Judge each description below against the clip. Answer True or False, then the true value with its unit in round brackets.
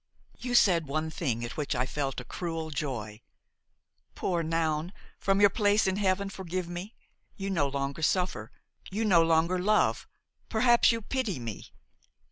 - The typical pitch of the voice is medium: True (170 Hz)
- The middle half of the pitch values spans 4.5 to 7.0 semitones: True (5.0 semitones)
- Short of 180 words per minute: True (155 wpm)